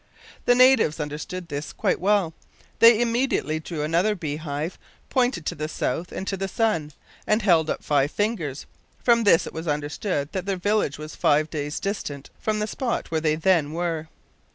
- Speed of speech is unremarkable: Yes, average, 180 wpm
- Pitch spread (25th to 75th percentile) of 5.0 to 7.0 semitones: Yes, wide, 5.5 semitones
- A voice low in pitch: No, medium, 170 Hz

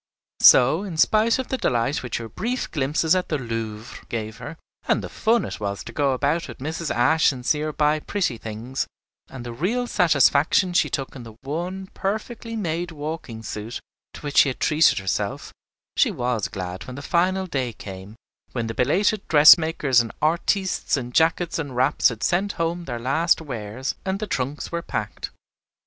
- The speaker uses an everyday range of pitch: No, wide, 6.0 semitones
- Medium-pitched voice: Yes, medium, 145 Hz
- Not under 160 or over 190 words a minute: Yes, average, 185 wpm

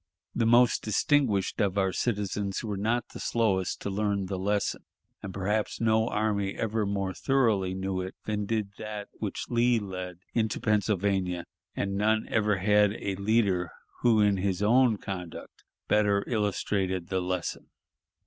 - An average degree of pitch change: No, narrow, 2.3 semitones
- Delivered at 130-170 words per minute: Yes, average, 150 wpm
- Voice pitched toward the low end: Yes, low, 100 Hz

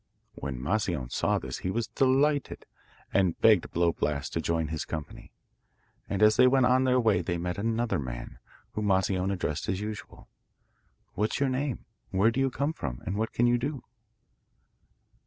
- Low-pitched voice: Yes, low, 100 Hz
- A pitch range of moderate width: No, wide, 6.7 semitones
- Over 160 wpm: Yes, average, 175 wpm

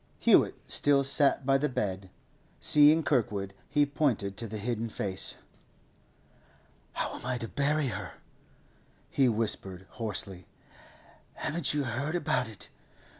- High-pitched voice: No, low, 125 Hz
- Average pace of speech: No, slow, 125 wpm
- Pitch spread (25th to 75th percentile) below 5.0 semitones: No, wide, 5.6 semitones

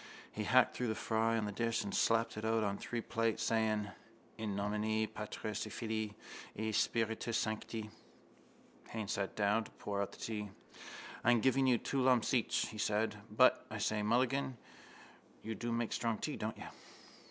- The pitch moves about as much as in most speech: No, narrow, 1.5 semitones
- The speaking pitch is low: Yes, low, 110 Hz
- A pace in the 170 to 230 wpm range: Yes, average, 175 wpm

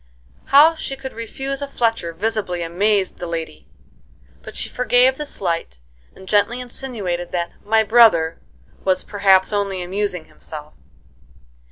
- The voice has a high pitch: Yes, high, 205 Hz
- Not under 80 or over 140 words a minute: Yes, slow, 135 wpm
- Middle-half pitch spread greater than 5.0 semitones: Yes, wide, 5.5 semitones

